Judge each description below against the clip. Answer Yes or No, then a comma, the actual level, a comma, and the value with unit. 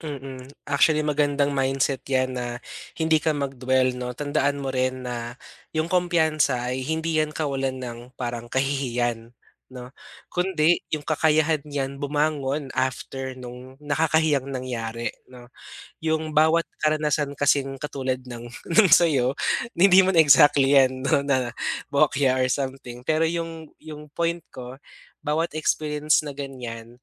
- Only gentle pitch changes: No, average, 3.1 semitones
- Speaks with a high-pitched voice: No, medium, 140 Hz